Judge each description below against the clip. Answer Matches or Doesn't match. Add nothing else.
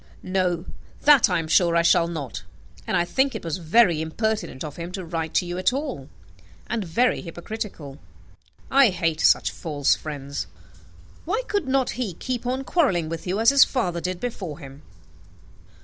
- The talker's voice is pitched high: Doesn't match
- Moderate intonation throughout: Doesn't match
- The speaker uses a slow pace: Doesn't match